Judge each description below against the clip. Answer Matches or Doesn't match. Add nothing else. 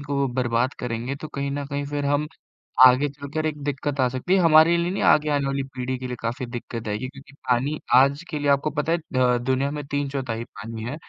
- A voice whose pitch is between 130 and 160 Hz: Matches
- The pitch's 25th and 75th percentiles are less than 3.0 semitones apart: Matches